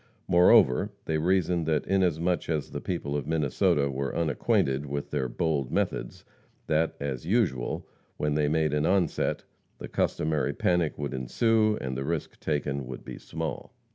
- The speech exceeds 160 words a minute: No, average, 155 wpm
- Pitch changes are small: No, average, 3.6 semitones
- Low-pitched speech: Yes, very low, 75 Hz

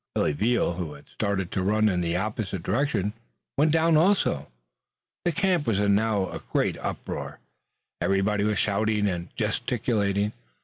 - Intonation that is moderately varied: Yes, average, 3.4 semitones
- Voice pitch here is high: No, low, 105 Hz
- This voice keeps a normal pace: Yes, average, 150 wpm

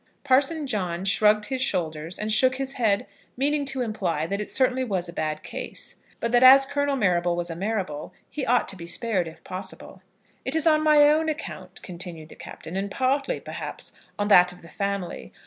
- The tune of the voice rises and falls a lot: Yes, wide, 7.1 semitones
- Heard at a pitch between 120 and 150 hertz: No, high, 210 Hz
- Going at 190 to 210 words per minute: Yes, average, 200 wpm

